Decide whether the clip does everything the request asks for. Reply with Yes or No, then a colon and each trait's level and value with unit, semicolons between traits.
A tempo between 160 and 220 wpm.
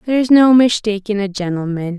No: average, 150 wpm